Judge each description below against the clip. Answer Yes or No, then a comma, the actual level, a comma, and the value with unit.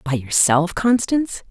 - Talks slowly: Yes, slow, 120 wpm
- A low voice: No, high, 190 Hz